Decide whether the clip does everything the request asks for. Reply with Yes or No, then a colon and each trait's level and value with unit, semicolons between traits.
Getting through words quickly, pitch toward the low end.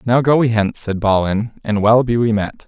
Yes: fast, 245 wpm; low, 110 Hz